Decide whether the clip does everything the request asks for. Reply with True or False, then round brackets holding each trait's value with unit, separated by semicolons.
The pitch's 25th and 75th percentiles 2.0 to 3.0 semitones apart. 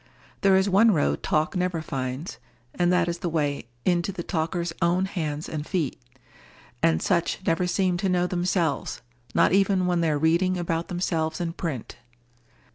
True (2.6 semitones)